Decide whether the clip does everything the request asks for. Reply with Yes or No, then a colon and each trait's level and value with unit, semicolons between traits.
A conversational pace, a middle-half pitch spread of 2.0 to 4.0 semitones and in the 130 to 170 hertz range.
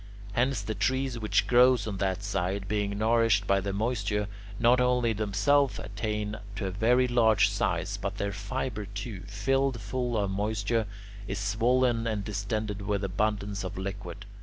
No: average, 160 wpm; average, 2.9 semitones; low, 105 Hz